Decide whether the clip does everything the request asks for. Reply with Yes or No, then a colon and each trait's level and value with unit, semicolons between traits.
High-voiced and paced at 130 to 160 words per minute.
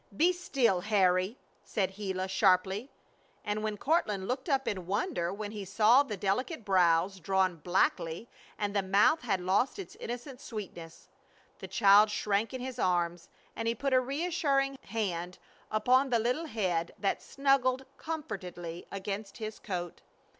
Yes: high, 210 Hz; average, 145 wpm